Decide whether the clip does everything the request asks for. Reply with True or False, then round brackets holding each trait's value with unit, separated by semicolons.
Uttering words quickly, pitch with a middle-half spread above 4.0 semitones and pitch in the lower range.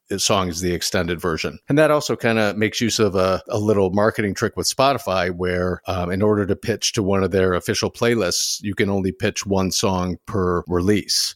False (210 wpm; 3.0 semitones; 100 Hz)